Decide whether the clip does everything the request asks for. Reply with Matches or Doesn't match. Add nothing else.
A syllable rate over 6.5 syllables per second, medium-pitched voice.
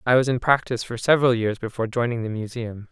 Doesn't match